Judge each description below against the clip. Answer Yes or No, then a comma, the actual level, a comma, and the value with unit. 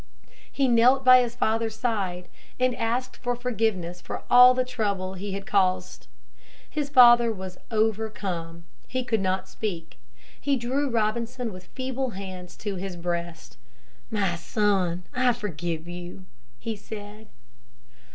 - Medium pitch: No, high, 215 Hz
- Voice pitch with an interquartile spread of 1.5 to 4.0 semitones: No, average, 4.8 semitones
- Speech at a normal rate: No, slow, 130 wpm